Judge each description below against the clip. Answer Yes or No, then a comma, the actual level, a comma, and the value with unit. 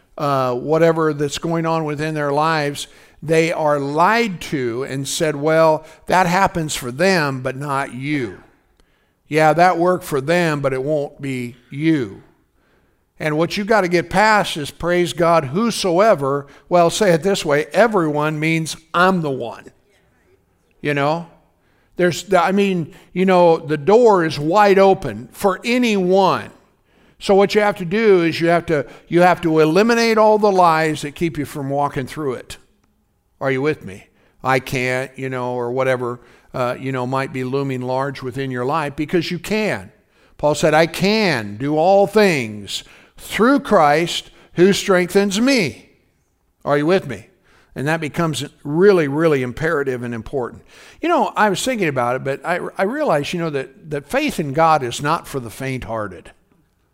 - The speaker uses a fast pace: No, average, 170 wpm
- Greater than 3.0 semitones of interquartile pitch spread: Yes, average, 4.8 semitones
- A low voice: No, medium, 160 Hz